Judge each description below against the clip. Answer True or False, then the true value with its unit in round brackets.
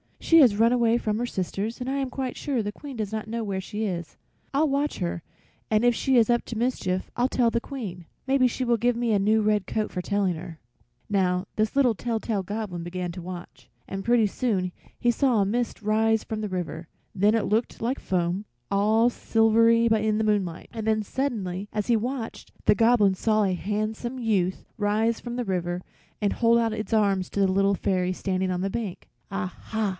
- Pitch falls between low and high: False (215 Hz)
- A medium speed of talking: False (215 wpm)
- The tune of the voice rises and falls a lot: False (3.4 semitones)